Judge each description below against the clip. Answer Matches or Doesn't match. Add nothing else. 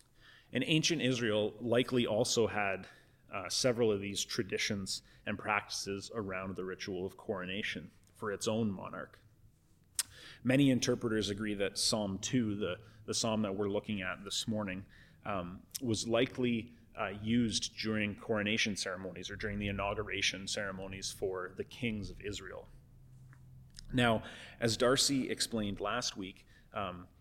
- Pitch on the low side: Matches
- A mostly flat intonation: Doesn't match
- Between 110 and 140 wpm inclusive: Matches